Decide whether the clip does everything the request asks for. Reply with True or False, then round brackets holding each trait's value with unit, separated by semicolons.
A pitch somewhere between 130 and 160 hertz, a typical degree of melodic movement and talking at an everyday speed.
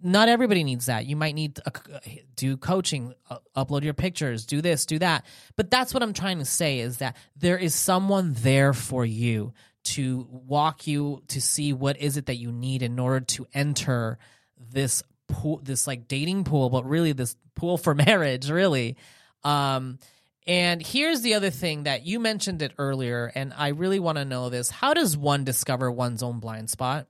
True (140 Hz; 4.2 semitones; 190 wpm)